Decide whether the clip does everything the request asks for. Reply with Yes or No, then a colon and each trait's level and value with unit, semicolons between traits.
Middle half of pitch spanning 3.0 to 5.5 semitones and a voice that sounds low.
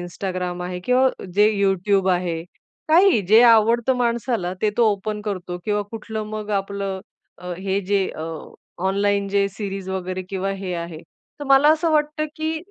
No: average, 3.6 semitones; high, 200 Hz